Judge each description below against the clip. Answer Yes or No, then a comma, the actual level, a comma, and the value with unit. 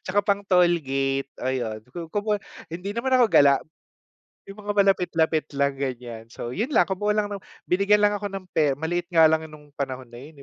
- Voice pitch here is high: No, medium, 170 Hz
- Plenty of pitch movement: Yes, wide, 6.7 semitones